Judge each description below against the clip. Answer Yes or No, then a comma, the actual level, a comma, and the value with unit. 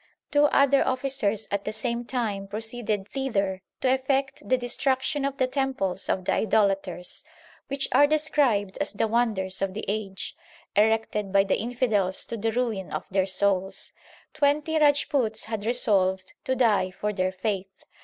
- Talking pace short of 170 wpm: Yes, average, 155 wpm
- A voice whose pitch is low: No, high, 220 Hz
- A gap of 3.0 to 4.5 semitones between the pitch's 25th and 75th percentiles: No, average, 5.0 semitones